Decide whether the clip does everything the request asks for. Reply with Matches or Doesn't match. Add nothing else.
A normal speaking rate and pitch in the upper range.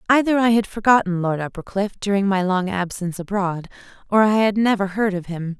Matches